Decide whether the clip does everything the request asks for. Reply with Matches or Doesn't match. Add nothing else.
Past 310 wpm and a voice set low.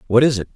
Matches